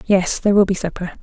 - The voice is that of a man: No, female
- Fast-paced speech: Yes, fast, 245 wpm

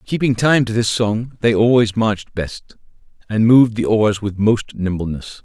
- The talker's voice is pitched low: Yes, low, 110 Hz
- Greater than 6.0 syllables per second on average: No, 4.6 syllables/s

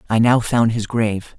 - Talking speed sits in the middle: No, fast, 215 wpm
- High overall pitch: No, low, 110 Hz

